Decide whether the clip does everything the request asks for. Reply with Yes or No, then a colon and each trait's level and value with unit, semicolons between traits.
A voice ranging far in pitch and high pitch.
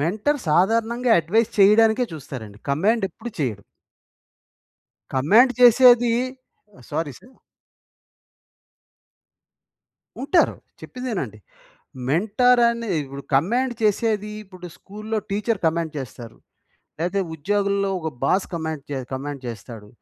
Yes: wide, 7.7 semitones; high, 200 Hz